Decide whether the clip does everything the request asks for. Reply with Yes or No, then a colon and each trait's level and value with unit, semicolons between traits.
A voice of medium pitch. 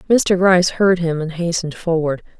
Yes: medium, 170 Hz